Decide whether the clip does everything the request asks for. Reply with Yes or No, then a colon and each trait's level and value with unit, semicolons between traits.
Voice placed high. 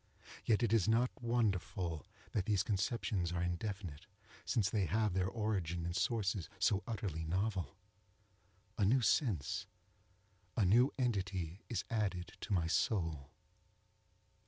No: very low, 95 Hz